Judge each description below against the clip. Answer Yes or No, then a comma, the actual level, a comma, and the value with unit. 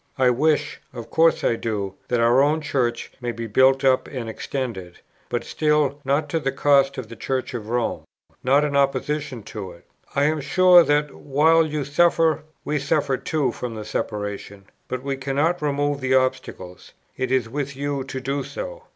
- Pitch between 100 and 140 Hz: Yes, low, 135 Hz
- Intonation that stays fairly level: No, average, 3.5 semitones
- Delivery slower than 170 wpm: No, average, 185 wpm